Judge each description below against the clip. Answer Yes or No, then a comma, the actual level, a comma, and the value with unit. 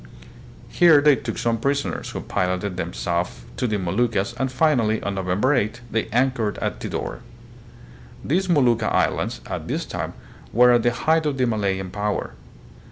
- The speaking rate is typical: Yes, average, 165 wpm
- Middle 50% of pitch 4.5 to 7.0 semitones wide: Yes, average, 4.8 semitones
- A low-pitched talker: Yes, low, 115 Hz